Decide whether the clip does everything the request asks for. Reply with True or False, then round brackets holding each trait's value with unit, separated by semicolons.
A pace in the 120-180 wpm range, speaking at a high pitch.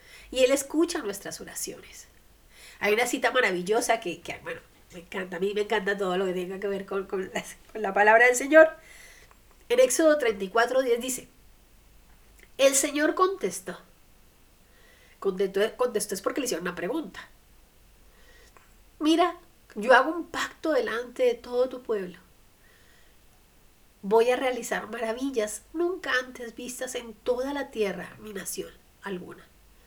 True (145 wpm; 235 Hz)